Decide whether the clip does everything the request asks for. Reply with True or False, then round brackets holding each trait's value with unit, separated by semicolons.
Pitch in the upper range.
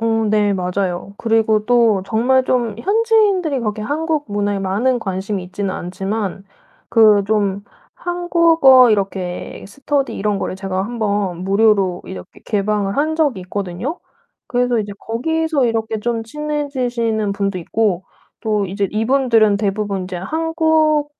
True (220 Hz)